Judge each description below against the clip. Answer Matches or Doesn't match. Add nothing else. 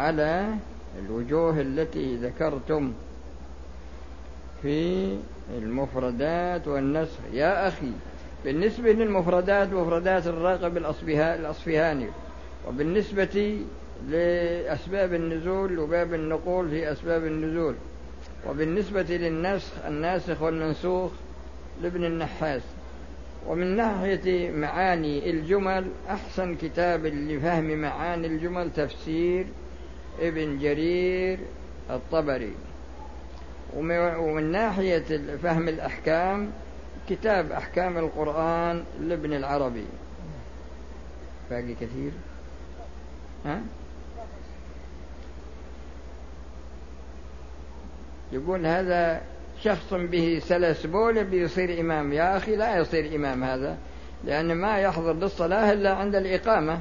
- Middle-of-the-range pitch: Matches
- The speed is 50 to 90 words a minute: Matches